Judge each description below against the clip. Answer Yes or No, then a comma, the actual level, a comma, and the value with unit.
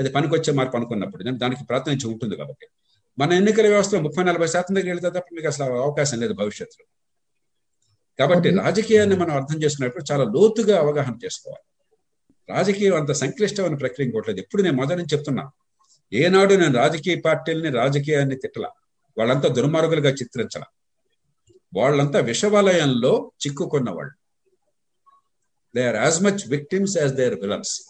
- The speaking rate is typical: No, fast, 135 wpm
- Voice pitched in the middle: Yes, medium, 160 Hz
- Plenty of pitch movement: Yes, wide, 6.3 semitones